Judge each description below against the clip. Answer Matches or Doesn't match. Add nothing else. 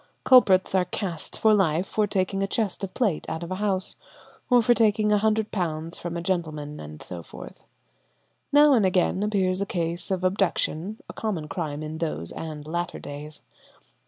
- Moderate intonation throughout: Matches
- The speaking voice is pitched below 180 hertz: Doesn't match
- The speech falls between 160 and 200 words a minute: Matches